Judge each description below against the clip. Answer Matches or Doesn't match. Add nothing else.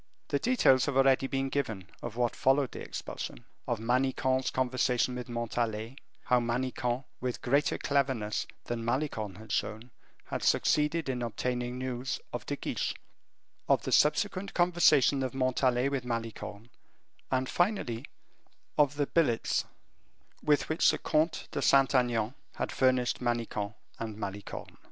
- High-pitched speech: Doesn't match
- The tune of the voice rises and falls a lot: Doesn't match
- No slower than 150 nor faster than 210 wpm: Doesn't match